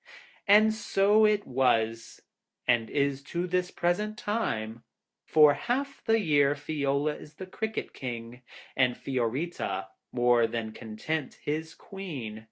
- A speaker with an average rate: No, slow, 125 wpm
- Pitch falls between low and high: Yes, medium, 145 Hz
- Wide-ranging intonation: Yes, wide, 8.1 semitones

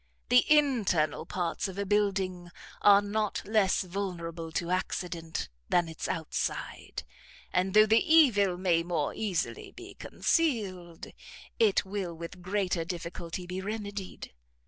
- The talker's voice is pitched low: No, high, 190 Hz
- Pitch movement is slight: No, average, 3.2 semitones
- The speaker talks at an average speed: No, slow, 125 wpm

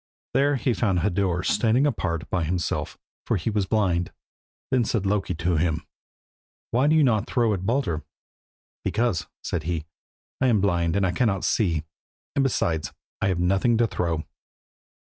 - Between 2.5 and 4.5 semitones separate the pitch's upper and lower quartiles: No, wide, 5.4 semitones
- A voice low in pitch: Yes, very low, 95 Hz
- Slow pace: No, average, 165 wpm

